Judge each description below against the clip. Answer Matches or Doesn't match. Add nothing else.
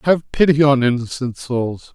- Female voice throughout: Doesn't match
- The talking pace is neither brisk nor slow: Matches